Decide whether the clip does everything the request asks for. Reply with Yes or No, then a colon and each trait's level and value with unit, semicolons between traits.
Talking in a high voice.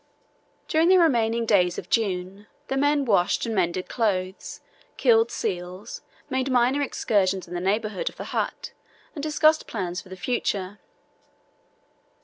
Yes: high, 215 Hz